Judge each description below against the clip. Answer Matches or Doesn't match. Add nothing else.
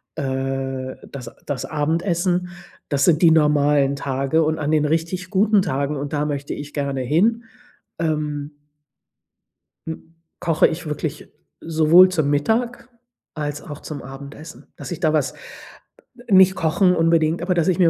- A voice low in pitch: Doesn't match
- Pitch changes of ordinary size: Matches